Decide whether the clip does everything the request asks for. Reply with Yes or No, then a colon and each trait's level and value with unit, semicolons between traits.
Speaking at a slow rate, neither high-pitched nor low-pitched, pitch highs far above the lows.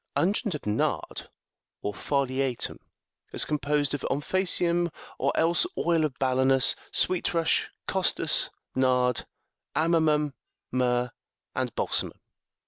No: slow, 105 wpm; medium, 145 Hz; average, 4.4 semitones